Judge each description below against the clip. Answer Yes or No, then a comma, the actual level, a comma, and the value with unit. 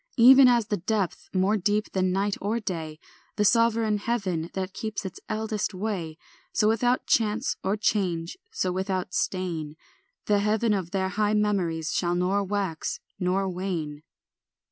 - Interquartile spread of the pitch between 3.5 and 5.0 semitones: No, average, 2.8 semitones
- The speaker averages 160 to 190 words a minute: No, average, 150 wpm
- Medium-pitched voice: No, high, 195 Hz